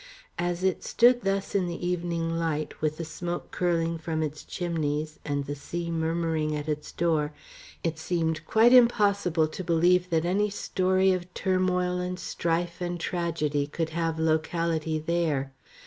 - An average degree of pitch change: No, narrow, 2.2 semitones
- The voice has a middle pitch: Yes, medium, 170 Hz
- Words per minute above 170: No, average, 155 wpm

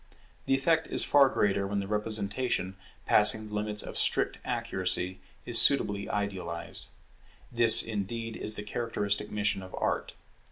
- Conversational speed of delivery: Yes, average, 145 wpm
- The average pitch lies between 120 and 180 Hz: No, low, 105 Hz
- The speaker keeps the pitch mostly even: Yes, narrow, 2.3 semitones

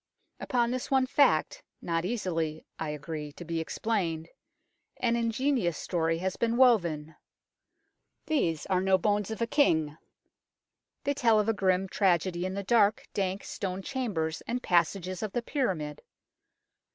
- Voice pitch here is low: No, high, 190 Hz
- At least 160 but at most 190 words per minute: No, average, 145 wpm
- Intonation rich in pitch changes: Yes, wide, 5.8 semitones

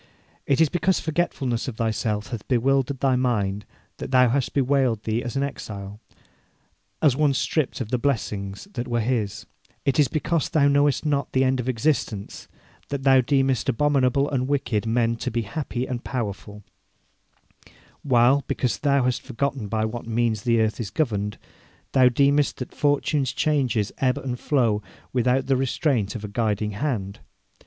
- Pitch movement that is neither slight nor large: Yes, average, 3.8 semitones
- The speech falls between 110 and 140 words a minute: No, average, 165 wpm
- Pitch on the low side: Yes, low, 125 Hz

